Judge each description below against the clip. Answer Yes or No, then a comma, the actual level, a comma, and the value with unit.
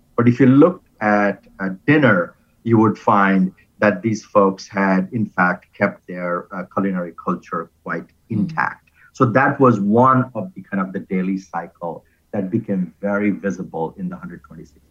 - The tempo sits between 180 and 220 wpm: No, average, 165 wpm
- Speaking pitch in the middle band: No, low, 100 Hz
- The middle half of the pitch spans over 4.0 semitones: No, average, 3.3 semitones